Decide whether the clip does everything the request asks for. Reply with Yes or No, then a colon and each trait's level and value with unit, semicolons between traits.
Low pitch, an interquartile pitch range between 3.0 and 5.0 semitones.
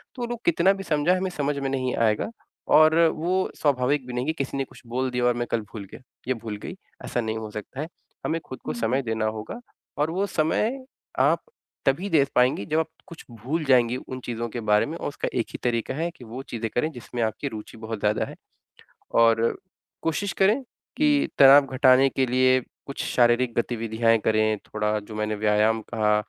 No: low, 125 Hz; wide, 5.5 semitones